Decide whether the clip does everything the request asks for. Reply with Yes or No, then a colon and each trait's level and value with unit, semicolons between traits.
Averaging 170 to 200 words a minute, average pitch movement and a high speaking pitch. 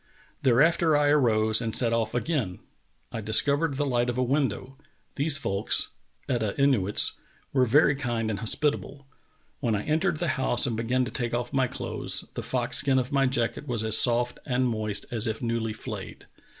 No: average, 180 wpm; average, 3.6 semitones; low, 125 Hz